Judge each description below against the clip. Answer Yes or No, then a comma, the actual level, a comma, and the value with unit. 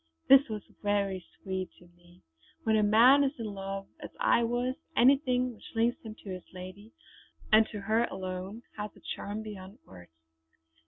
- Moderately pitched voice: No, high, 210 Hz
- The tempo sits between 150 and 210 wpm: Yes, average, 170 wpm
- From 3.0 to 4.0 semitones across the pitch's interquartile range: Yes, average, 3.6 semitones